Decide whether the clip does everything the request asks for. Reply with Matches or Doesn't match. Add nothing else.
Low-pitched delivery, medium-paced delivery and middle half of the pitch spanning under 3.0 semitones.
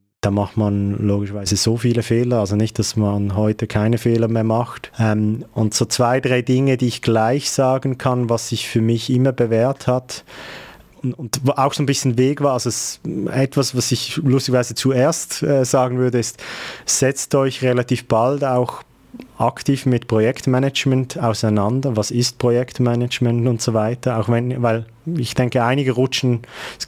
Matches